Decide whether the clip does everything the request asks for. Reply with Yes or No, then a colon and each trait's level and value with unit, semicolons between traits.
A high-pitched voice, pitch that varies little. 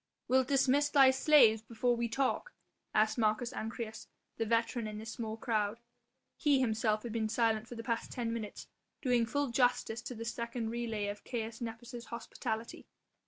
Yes: high, 230 Hz; narrow, 2.0 semitones